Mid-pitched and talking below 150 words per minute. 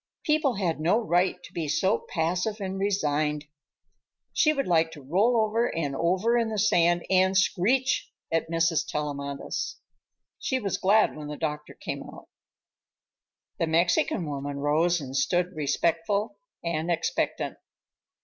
Yes: medium, 175 Hz; average, 140 wpm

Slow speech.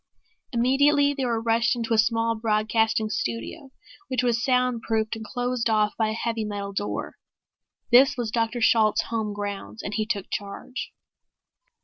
No: average, 150 wpm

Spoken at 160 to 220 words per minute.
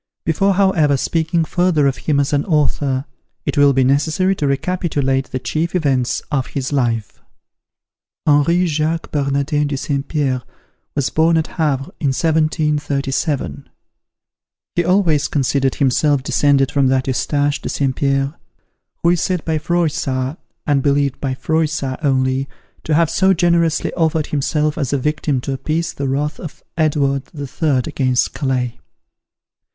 No: average, 150 wpm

